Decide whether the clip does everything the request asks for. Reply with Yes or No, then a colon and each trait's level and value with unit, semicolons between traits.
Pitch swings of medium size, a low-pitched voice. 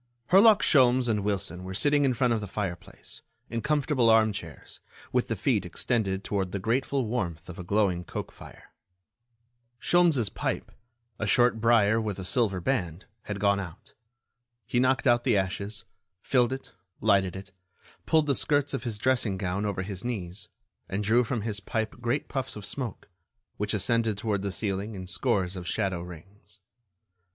Yes: average, 4.1 semitones; low, 105 Hz